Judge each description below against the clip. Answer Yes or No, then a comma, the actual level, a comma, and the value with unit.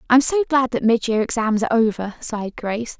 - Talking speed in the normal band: No, fast, 220 wpm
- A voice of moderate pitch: No, high, 235 Hz